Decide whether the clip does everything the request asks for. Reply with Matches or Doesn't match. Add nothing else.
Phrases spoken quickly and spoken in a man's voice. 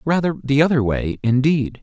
Doesn't match